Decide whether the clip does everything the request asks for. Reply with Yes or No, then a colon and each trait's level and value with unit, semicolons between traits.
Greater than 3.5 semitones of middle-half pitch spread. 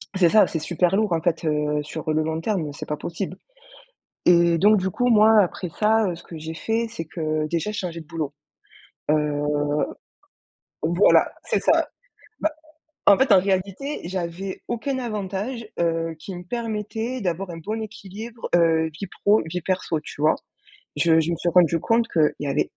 Yes: average, 4.6 semitones